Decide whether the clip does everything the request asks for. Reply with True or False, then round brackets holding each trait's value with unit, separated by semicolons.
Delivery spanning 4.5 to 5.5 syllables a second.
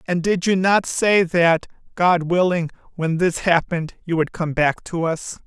False (4.3 syllables/s)